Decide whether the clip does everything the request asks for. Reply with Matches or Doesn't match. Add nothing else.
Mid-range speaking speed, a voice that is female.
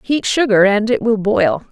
Doesn't match